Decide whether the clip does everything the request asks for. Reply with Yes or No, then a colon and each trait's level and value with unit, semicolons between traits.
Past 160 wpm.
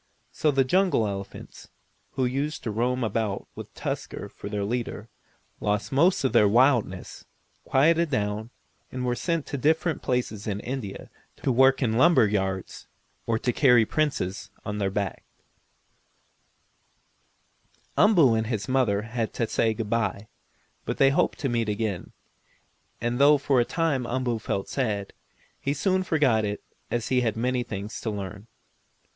No: average, 155 wpm